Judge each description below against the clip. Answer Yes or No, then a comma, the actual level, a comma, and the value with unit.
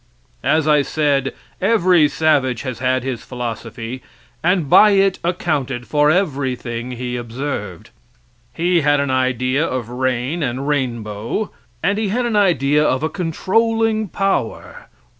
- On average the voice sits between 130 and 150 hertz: Yes, medium, 140 Hz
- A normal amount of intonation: No, wide, 5.7 semitones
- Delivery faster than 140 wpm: No, slow, 135 wpm